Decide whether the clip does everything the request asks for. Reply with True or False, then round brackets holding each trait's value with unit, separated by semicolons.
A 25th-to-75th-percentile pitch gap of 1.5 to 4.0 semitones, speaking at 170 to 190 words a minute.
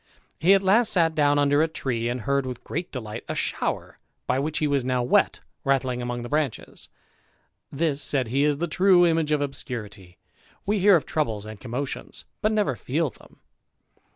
False (4.6 semitones; 185 wpm)